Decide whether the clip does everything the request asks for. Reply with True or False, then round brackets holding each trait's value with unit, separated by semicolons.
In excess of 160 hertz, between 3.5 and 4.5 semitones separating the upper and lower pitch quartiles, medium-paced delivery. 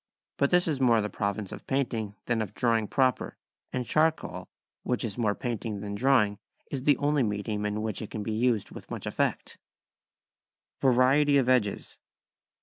False (115 Hz; 4.2 semitones; 175 wpm)